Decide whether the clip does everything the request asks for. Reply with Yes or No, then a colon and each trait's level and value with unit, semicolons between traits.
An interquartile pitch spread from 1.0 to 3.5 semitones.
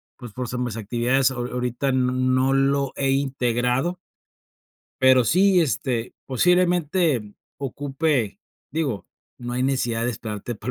Yes: narrow, 2.4 semitones